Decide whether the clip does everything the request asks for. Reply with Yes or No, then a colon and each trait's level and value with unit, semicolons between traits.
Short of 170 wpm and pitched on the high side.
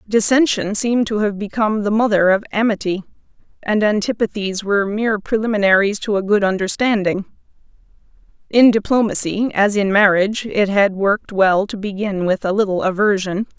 Yes: average, 145 wpm; high, 205 Hz